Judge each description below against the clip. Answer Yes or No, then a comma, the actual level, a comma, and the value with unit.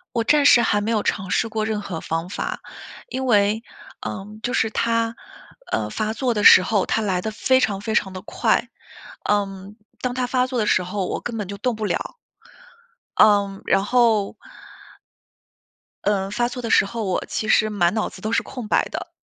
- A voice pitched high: Yes, high, 215 Hz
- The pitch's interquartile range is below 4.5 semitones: Yes, average, 2.7 semitones